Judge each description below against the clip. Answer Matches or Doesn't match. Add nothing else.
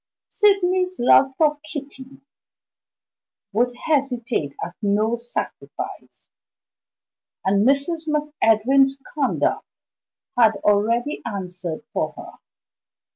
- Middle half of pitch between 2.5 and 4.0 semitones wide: Doesn't match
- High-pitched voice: Matches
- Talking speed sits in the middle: Doesn't match